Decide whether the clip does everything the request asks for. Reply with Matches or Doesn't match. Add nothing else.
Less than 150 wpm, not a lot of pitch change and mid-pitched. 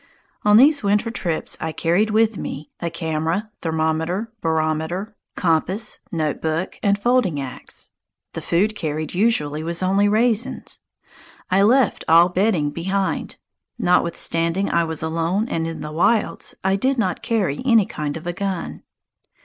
Doesn't match